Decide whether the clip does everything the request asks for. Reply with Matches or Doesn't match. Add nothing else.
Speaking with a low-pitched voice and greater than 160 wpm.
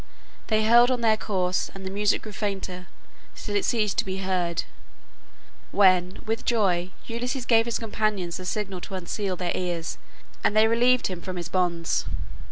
Doesn't match